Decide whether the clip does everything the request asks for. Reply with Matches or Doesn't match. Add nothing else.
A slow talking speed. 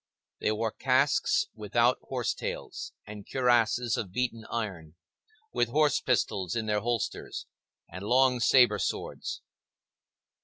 Matches